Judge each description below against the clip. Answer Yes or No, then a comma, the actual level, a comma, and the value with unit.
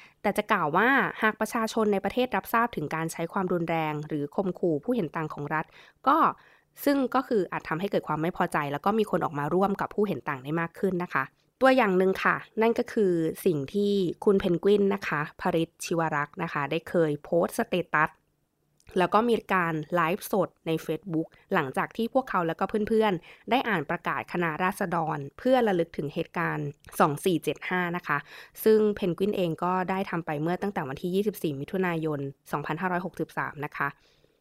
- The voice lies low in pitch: No, medium, 180 Hz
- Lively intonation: No, average, 4.1 semitones